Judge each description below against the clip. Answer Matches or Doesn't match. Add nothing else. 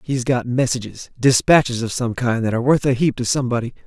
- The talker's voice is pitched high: Doesn't match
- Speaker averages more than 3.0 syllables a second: Matches